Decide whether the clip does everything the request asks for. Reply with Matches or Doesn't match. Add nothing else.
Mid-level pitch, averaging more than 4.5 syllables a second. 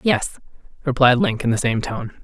Matches